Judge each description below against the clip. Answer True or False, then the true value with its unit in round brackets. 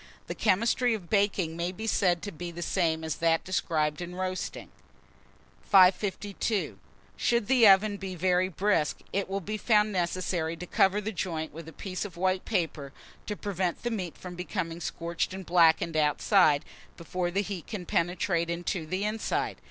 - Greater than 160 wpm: True (170 wpm)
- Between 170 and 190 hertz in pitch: True (185 Hz)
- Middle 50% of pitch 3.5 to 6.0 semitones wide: False (3.1 semitones)